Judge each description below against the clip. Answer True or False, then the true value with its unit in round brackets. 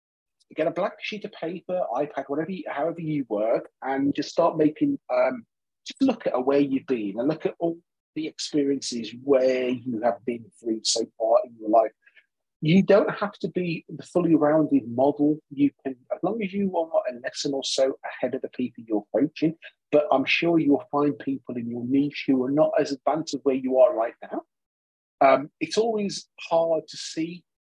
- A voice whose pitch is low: False (150 Hz)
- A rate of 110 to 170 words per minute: False (195 wpm)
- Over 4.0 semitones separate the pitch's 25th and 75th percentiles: True (4.5 semitones)